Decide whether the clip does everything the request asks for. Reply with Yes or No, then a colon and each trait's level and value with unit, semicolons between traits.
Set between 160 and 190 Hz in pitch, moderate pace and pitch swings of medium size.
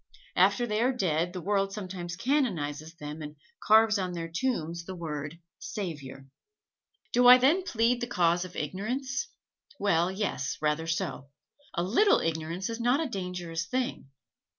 No: medium, 185 Hz; average, 150 wpm; wide, 6.2 semitones